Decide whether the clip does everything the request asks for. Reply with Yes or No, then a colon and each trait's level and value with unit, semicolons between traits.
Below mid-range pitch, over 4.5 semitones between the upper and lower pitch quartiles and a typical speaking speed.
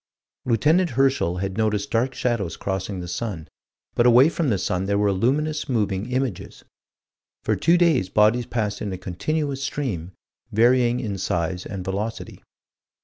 Yes: low, 110 Hz; average, 5.3 semitones; average, 150 wpm